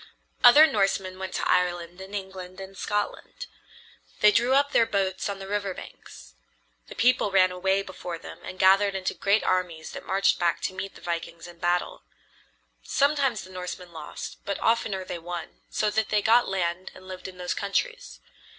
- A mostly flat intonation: Yes, narrow, 2.3 semitones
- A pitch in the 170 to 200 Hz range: Yes, high, 190 Hz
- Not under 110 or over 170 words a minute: No, average, 180 wpm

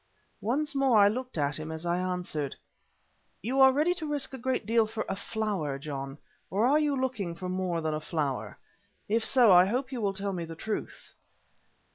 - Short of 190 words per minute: No, average, 200 wpm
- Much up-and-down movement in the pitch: Yes, wide, 7.4 semitones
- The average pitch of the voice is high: Yes, high, 205 Hz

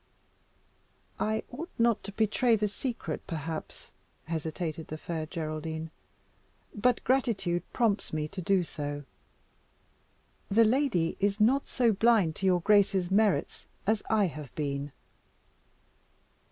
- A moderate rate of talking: No, slow, 120 wpm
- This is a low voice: No, high, 195 Hz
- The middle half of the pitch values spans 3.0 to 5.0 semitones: No, wide, 5.6 semitones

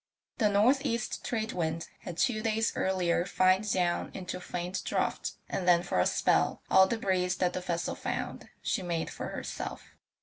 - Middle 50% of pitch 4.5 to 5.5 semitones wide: No, average, 3.3 semitones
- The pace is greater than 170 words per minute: Yes, average, 180 wpm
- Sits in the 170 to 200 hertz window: Yes, medium, 185 Hz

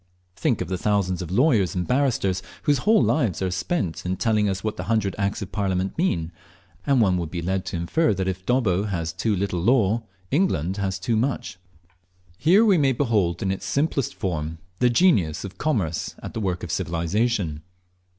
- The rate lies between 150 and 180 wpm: No, average, 190 wpm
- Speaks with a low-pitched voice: Yes, low, 100 Hz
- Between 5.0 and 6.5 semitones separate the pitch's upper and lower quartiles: Yes, average, 5.3 semitones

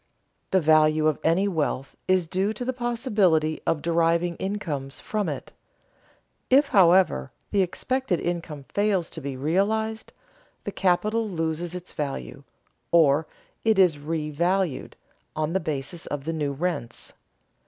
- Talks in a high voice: No, medium, 170 Hz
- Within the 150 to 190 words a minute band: No, slow, 135 wpm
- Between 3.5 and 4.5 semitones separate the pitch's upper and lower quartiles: Yes, average, 4.1 semitones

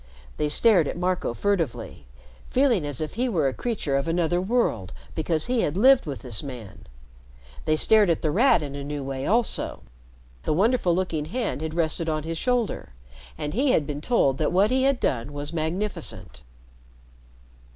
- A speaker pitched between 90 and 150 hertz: No, medium, 165 Hz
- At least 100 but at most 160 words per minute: No, average, 180 wpm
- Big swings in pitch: Yes, wide, 6.7 semitones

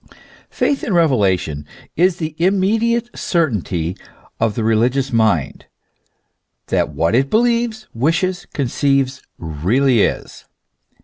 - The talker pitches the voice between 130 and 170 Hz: Yes, low, 135 Hz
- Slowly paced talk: Yes, slow, 105 wpm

